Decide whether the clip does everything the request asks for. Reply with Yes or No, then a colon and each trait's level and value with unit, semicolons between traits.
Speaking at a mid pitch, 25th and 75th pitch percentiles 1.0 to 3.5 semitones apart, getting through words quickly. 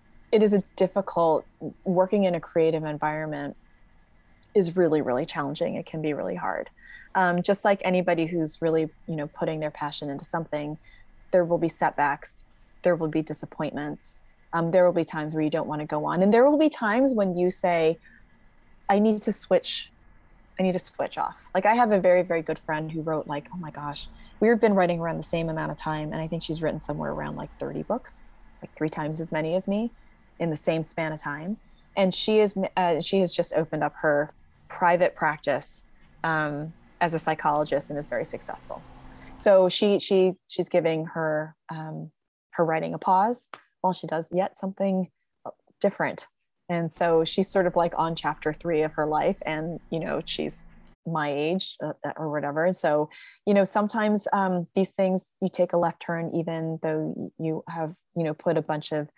No: medium, 165 Hz; average, 3.1 semitones; average, 195 wpm